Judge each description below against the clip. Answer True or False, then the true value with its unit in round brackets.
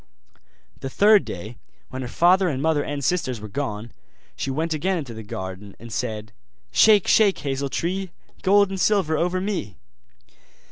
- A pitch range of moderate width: False (8.2 semitones)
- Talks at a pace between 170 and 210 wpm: False (160 wpm)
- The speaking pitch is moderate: True (145 Hz)